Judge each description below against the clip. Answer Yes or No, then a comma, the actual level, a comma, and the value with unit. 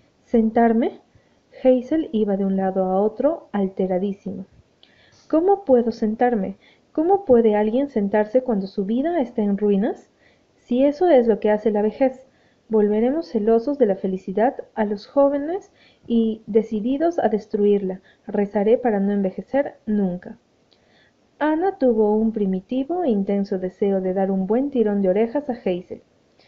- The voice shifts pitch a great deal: No, average, 4.1 semitones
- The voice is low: No, high, 220 Hz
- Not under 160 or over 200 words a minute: No, average, 145 wpm